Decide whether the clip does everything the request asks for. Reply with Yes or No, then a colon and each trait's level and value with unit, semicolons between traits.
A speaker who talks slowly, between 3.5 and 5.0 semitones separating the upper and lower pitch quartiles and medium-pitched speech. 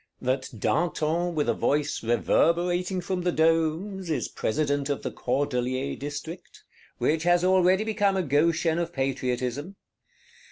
Yes: slow, 130 wpm; average, 3.9 semitones; medium, 160 Hz